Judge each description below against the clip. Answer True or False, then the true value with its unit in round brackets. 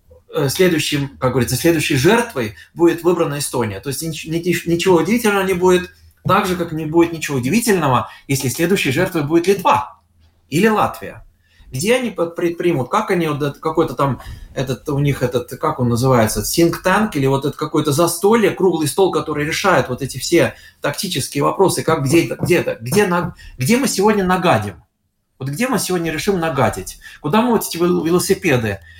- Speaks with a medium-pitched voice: True (160 Hz)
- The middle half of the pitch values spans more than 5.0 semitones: True (5.6 semitones)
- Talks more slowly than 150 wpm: False (155 wpm)